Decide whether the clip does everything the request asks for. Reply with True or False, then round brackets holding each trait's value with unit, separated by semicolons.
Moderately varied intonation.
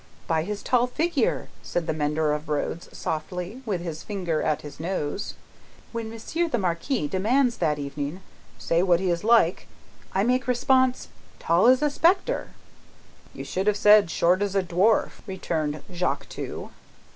False (6.2 semitones)